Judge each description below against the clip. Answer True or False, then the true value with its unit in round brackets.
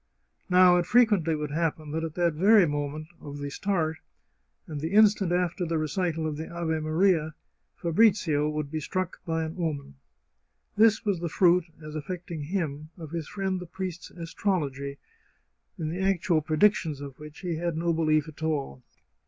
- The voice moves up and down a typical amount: True (3.0 semitones)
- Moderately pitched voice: True (165 Hz)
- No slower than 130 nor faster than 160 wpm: False (170 wpm)